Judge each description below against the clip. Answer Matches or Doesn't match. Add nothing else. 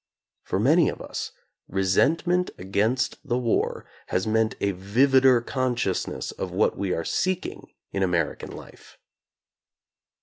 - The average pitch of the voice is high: Doesn't match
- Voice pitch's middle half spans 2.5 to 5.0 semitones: Doesn't match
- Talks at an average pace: Doesn't match